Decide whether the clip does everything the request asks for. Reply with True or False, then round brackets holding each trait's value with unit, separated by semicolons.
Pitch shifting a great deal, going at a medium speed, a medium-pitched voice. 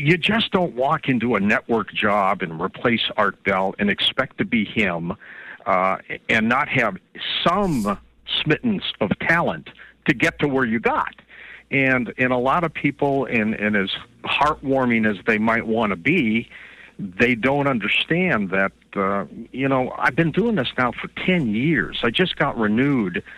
False (6.2 semitones; 170 wpm; 130 Hz)